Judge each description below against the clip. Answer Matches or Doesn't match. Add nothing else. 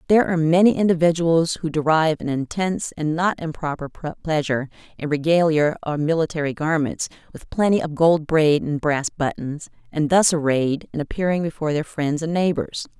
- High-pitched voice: Doesn't match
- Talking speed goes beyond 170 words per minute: Doesn't match